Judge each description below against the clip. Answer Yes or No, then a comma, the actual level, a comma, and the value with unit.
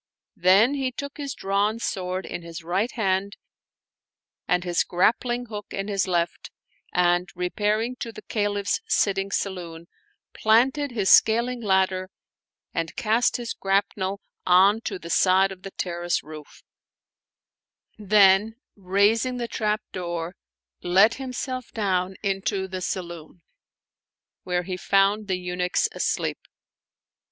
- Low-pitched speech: No, high, 195 Hz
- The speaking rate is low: Yes, slow, 125 wpm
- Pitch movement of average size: Yes, average, 3.3 semitones